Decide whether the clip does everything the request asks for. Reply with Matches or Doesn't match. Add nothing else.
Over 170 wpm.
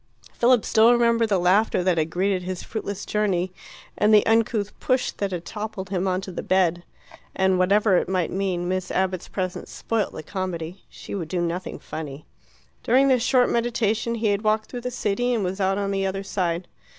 Matches